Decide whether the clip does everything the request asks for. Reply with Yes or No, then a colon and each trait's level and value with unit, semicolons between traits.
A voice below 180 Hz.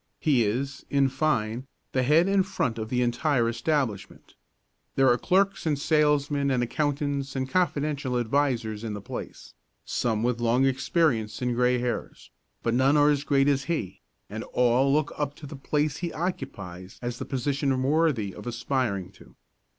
Yes: low, 135 Hz